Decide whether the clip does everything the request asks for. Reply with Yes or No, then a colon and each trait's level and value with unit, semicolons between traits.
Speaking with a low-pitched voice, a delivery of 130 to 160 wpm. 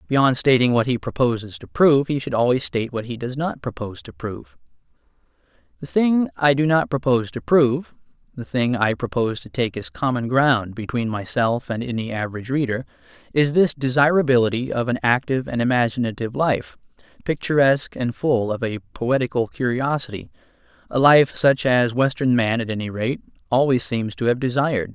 No: low, 125 Hz; average, 170 wpm